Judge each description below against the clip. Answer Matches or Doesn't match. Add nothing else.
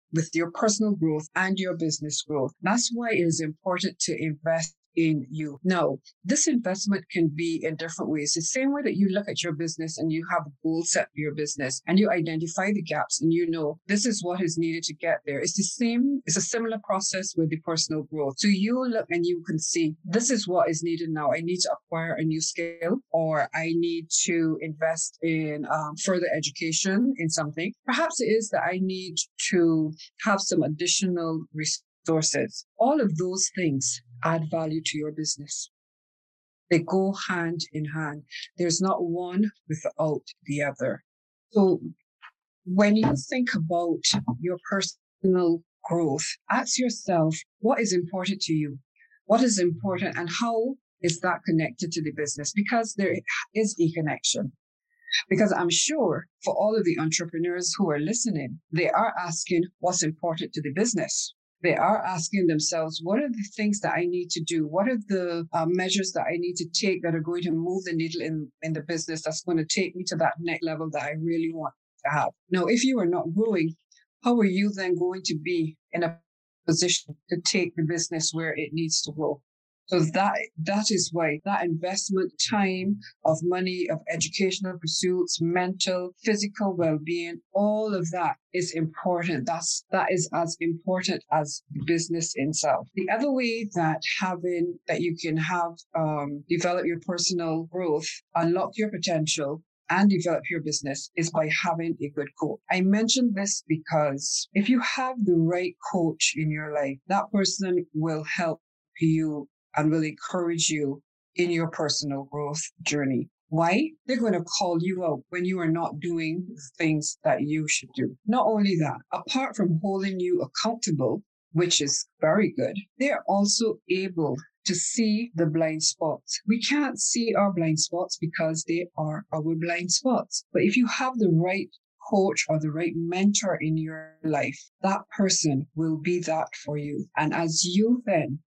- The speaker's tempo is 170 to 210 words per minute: Matches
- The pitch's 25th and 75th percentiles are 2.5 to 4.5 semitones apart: Matches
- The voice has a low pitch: Doesn't match